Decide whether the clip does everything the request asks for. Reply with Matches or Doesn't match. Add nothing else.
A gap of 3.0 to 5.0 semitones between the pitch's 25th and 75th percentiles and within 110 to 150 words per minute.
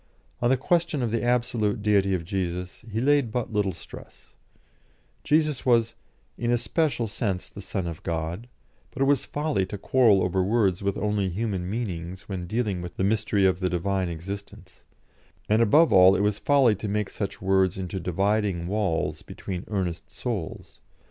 Doesn't match